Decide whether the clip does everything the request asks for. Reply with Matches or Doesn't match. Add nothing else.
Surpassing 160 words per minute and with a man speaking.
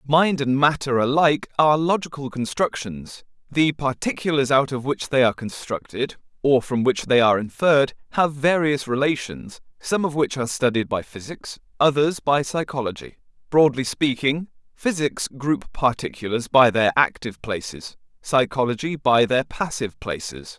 Doesn't match